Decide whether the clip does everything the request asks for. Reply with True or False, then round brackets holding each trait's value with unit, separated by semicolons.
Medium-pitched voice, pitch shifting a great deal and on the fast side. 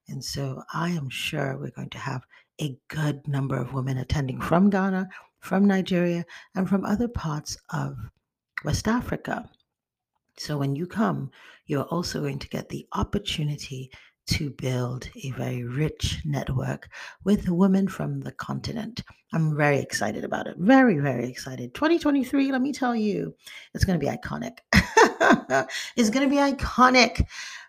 False (155 Hz; 6.9 semitones; 155 wpm)